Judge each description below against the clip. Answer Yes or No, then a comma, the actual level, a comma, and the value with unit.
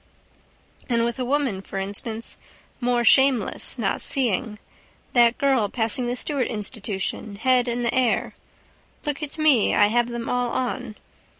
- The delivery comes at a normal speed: Yes, average, 145 wpm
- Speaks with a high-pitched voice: Yes, high, 240 Hz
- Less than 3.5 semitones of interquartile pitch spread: Yes, average, 2.7 semitones